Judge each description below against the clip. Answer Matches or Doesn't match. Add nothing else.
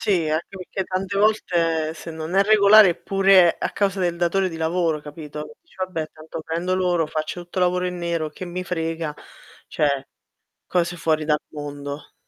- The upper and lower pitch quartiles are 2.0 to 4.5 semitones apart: Matches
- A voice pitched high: Doesn't match